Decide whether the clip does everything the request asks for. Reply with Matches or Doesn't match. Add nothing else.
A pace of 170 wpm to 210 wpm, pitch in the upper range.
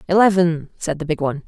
Doesn't match